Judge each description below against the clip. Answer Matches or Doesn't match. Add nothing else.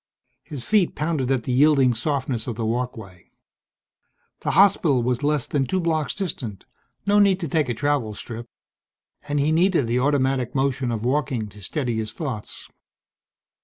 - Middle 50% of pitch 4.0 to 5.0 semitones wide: Matches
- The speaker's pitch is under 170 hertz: Matches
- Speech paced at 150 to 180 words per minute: Matches